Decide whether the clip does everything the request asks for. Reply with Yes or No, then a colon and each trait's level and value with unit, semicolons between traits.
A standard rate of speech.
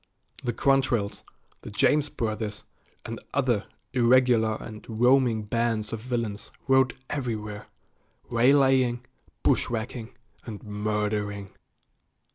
No: slow, 90 wpm